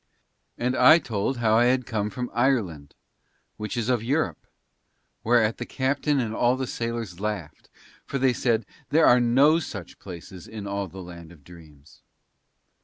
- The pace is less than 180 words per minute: Yes, average, 160 wpm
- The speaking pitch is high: No, low, 115 Hz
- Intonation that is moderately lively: Yes, average, 4.6 semitones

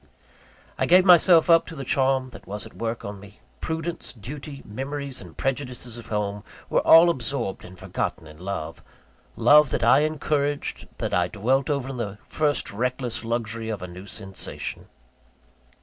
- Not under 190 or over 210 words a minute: No, average, 165 wpm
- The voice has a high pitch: No, low, 125 Hz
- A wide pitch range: Yes, wide, 5.7 semitones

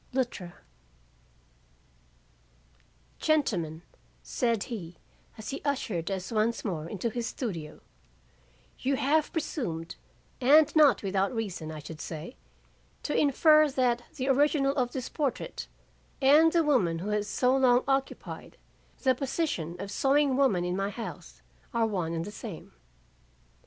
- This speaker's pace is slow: Yes, slow, 130 wpm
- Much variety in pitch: Yes, wide, 7.1 semitones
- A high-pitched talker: Yes, high, 235 Hz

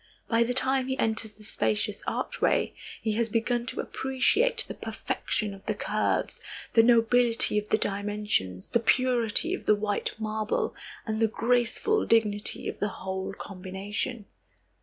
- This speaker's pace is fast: No, average, 150 wpm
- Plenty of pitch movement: No, average, 2.8 semitones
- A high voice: Yes, high, 220 Hz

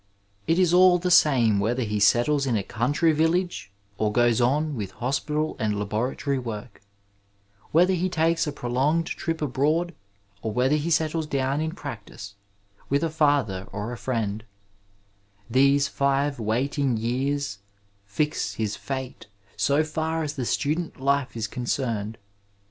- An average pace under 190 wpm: Yes, average, 150 wpm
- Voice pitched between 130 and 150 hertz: Yes, low, 135 Hz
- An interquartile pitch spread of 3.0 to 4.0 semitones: No, wide, 5.5 semitones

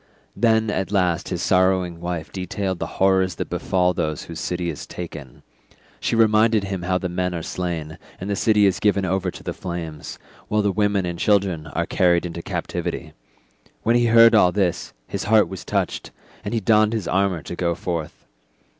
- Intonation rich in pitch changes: No, average, 2.9 semitones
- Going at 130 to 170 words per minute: No, average, 190 wpm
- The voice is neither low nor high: No, very low, 95 Hz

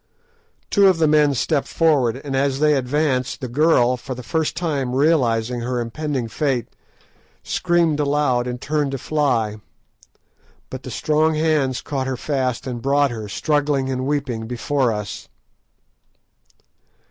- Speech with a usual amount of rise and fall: Yes, average, 3.3 semitones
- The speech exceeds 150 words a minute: No, average, 145 wpm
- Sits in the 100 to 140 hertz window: Yes, low, 135 Hz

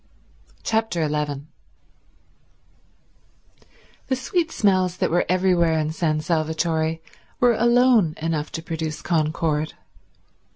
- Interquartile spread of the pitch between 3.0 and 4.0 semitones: Yes, average, 3.5 semitones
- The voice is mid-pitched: Yes, medium, 165 Hz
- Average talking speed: No, slow, 95 wpm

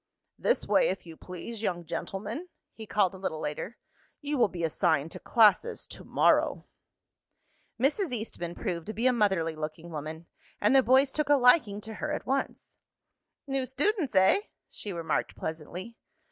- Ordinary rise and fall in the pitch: No, wide, 7.6 semitones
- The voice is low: No, high, 210 Hz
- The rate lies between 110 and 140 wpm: No, average, 165 wpm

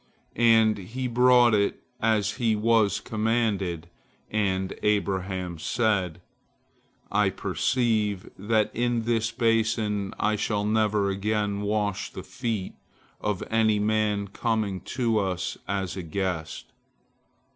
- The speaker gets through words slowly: Yes, slow, 115 wpm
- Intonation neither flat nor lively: No, narrow, 2.3 semitones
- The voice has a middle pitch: No, low, 105 Hz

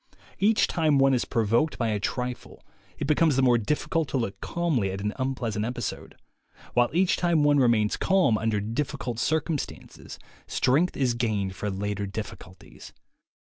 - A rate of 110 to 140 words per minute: No, average, 160 wpm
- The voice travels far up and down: Yes, wide, 5.7 semitones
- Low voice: Yes, low, 125 Hz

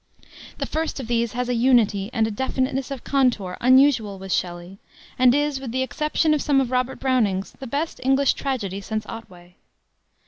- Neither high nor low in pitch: No, very high, 250 Hz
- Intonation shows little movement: No, average, 4.5 semitones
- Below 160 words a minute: No, average, 180 wpm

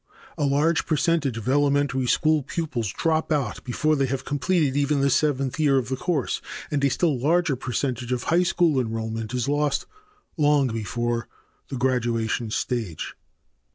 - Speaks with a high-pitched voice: No, low, 135 Hz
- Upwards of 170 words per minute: No, average, 155 wpm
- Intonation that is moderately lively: Yes, average, 3.6 semitones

